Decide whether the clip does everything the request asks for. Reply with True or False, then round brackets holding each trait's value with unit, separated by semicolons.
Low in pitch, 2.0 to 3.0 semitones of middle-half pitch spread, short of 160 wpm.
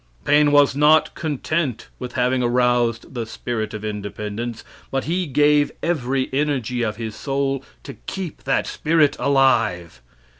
False (130 Hz; 3.9 semitones; 140 wpm)